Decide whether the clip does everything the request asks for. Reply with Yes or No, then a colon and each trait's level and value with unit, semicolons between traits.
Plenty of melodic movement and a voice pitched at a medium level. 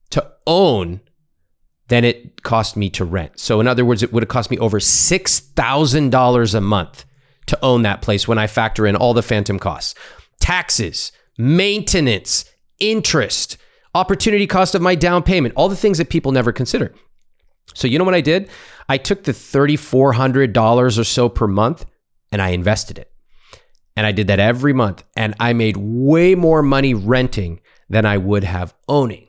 No: wide, 5.9 semitones; low, 120 Hz